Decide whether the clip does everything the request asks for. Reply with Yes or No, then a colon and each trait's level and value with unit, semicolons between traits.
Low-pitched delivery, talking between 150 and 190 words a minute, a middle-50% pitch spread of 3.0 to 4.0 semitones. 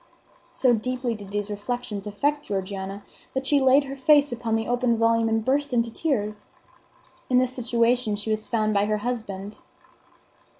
No: high, 230 Hz; average, 165 wpm; average, 3.4 semitones